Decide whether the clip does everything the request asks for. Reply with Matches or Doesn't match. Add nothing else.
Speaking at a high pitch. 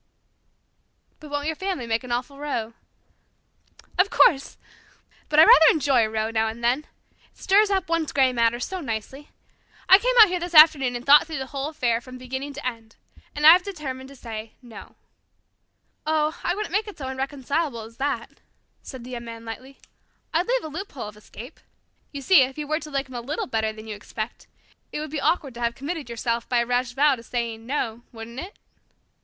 Matches